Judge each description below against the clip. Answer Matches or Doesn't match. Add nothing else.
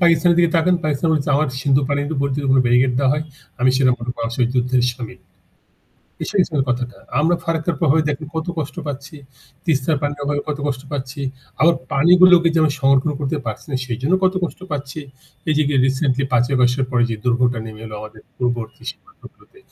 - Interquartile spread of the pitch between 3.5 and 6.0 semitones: Matches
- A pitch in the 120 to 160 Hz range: Matches